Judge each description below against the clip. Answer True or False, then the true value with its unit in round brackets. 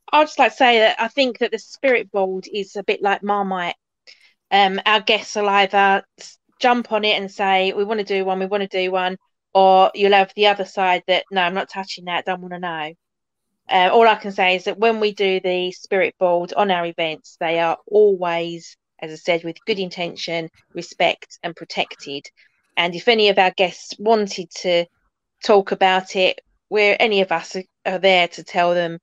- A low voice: False (190 Hz)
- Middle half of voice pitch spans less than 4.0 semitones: True (2.7 semitones)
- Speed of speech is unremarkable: False (210 wpm)